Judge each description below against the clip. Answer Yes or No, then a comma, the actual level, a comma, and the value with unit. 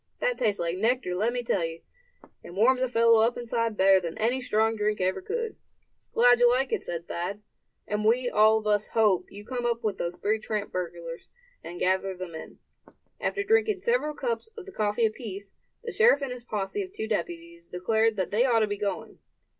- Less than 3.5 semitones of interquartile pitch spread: No, average, 4.3 semitones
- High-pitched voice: Yes, high, 220 Hz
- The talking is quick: Yes, fast, 210 wpm